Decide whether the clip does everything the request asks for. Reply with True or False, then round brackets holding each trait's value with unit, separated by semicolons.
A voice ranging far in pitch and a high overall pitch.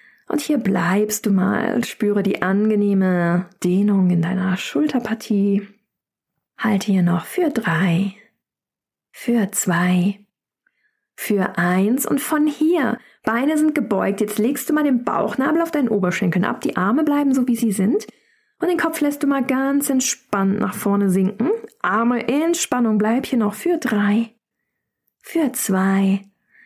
True (6.5 semitones; 220 Hz)